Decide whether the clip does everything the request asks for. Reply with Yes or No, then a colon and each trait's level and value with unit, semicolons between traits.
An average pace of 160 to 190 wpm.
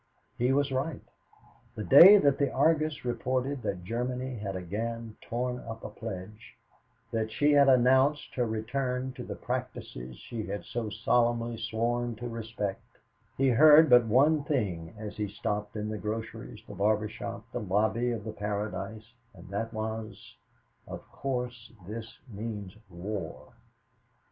No: average, 150 wpm